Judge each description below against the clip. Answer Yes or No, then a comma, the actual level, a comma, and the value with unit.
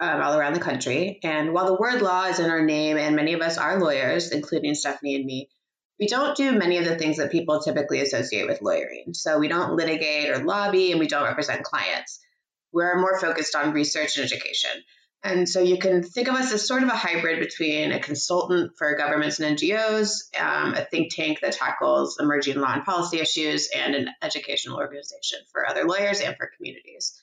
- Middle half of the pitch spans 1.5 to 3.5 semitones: No, average, 4.1 semitones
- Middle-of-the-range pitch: Yes, medium, 165 Hz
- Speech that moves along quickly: Yes, fast, 210 wpm